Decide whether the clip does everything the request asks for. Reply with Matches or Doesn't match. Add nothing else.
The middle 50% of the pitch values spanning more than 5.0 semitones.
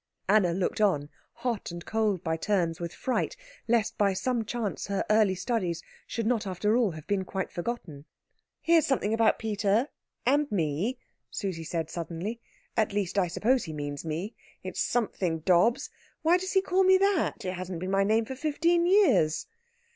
Matches